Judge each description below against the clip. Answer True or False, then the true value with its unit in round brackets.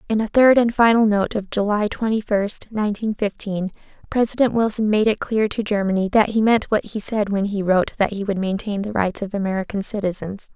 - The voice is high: True (210 Hz)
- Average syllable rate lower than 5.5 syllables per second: False (5.6 syllables/s)